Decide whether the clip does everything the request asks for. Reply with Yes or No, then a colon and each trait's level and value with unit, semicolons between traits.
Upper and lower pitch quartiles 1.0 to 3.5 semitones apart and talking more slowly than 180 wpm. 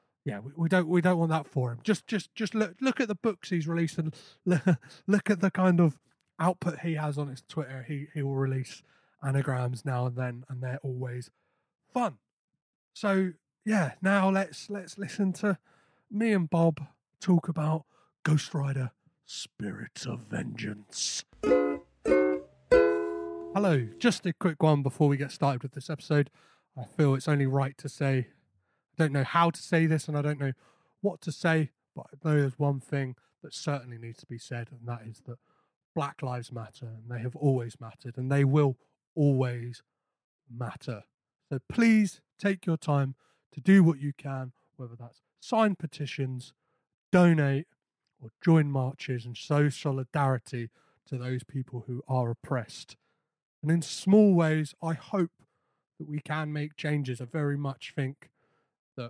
No: average, 4.5 semitones; average, 170 wpm